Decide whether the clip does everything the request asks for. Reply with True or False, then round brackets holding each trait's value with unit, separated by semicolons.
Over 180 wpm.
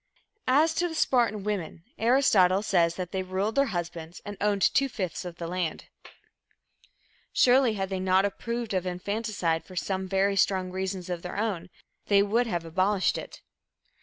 False (165 wpm)